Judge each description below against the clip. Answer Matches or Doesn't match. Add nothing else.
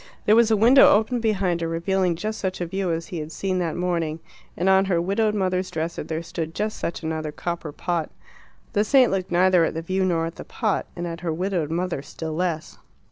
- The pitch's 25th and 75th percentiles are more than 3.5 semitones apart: Doesn't match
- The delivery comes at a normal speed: Doesn't match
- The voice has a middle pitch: Matches